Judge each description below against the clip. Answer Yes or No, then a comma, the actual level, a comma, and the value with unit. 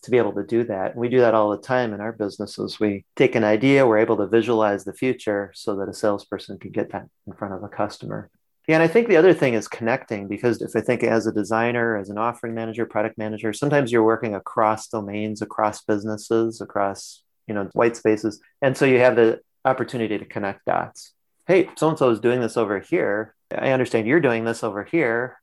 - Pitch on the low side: Yes, low, 110 Hz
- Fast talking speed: Yes, fast, 225 wpm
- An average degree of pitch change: No, narrow, 2.3 semitones